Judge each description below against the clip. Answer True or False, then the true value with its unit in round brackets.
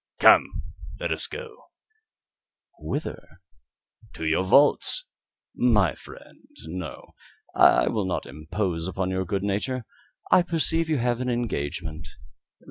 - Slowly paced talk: True (120 wpm)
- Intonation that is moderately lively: False (7.1 semitones)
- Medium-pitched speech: False (100 Hz)